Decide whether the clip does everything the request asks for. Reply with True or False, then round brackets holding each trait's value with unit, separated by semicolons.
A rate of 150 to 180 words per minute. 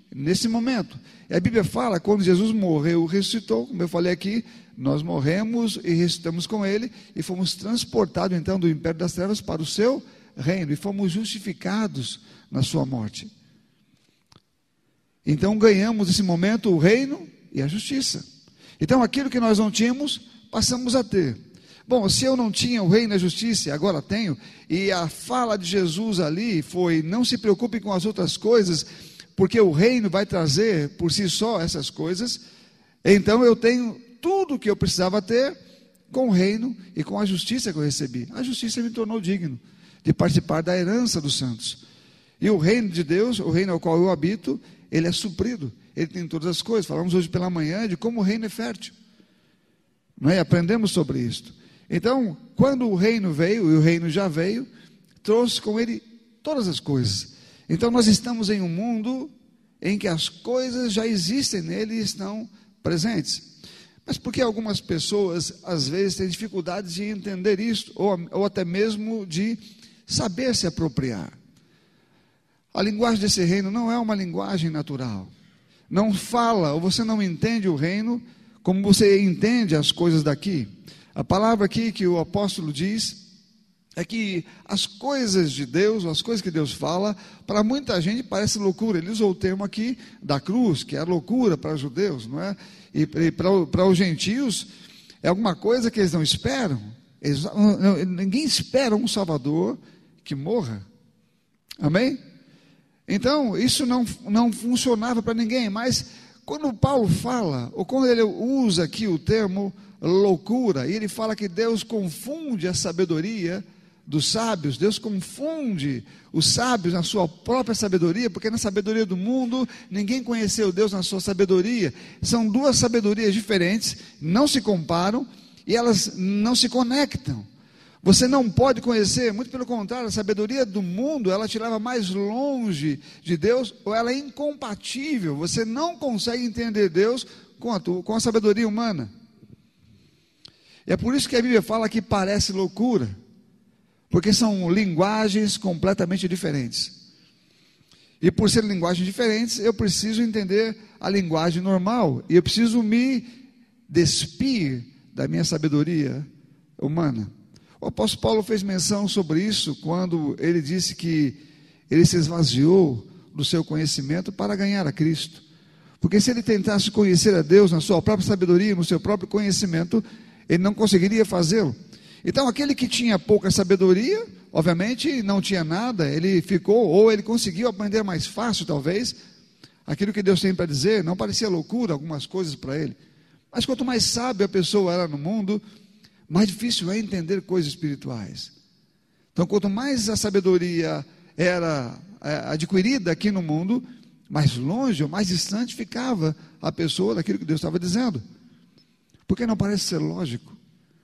True (160 wpm)